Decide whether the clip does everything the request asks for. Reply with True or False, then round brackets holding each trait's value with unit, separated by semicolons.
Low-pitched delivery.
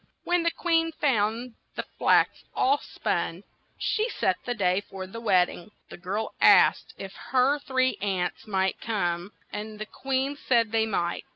False (220 Hz)